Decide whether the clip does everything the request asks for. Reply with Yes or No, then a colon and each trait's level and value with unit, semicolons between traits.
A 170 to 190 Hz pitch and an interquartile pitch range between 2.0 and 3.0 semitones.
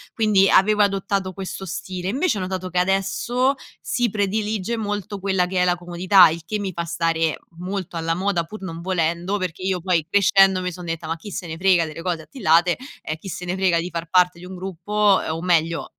Yes: medium, 185 Hz; narrow, 2.6 semitones